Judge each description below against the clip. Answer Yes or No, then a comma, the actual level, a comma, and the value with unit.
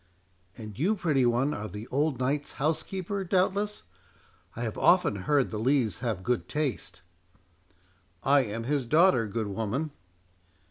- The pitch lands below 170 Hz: Yes, low, 135 Hz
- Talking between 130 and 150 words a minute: Yes, average, 145 wpm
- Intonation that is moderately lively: No, wide, 5.9 semitones